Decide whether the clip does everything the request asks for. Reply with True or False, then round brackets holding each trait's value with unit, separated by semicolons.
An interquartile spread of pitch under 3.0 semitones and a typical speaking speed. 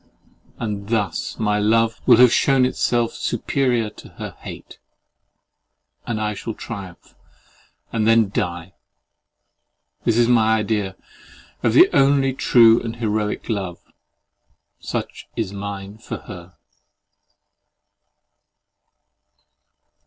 False (2.6 semitones; 105 wpm)